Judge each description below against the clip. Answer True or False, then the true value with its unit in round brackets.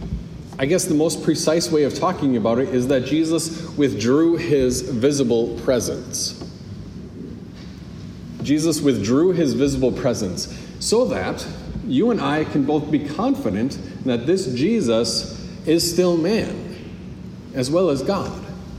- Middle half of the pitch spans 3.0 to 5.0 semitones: True (4.2 semitones)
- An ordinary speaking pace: False (130 wpm)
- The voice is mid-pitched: True (145 Hz)